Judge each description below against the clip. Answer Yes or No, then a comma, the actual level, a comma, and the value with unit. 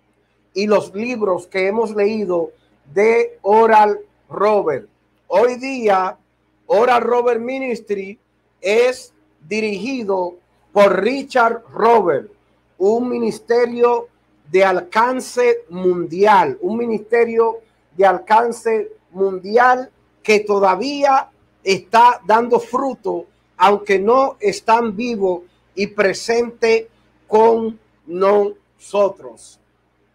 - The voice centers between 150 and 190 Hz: No, high, 220 Hz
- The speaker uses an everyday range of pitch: Yes, average, 3.5 semitones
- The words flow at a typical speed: No, slow, 85 wpm